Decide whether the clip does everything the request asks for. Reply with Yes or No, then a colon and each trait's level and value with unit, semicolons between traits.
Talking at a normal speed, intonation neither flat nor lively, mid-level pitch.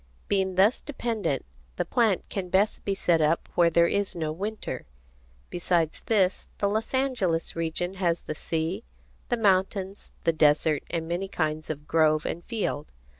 Yes: average, 160 wpm; average, 3.8 semitones; medium, 180 Hz